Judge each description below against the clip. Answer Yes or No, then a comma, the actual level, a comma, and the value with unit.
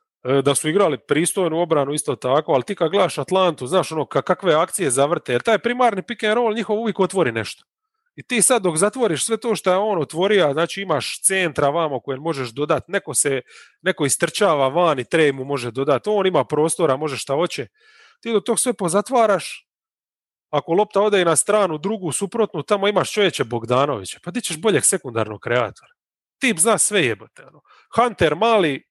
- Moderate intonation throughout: No, wide, 6.0 semitones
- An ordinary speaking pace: Yes, average, 190 wpm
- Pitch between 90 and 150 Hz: No, medium, 185 Hz